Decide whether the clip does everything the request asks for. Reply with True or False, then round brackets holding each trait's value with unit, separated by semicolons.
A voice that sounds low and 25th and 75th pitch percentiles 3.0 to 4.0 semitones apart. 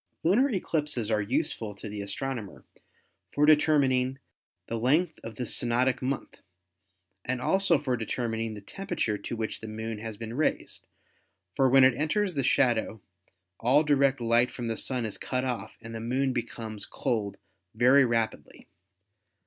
True (125 Hz; 3.6 semitones)